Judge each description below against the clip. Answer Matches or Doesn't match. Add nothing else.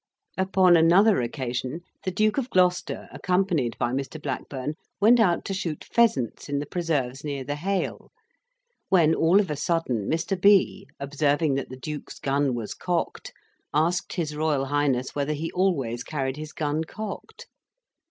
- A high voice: Doesn't match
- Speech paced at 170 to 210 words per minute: Doesn't match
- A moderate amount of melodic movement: Matches